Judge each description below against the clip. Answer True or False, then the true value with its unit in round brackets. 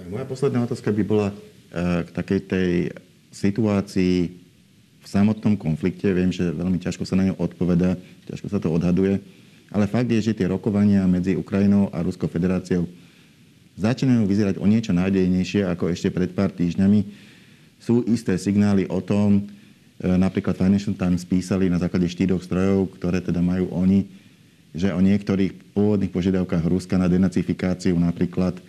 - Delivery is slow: False (150 wpm)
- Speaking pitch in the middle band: False (95 Hz)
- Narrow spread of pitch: True (2.0 semitones)